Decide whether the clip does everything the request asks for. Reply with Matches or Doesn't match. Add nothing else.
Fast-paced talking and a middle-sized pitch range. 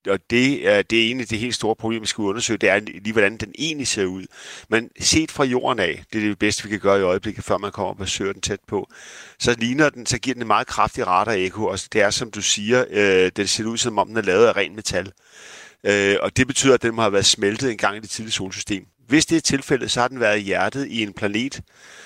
Matches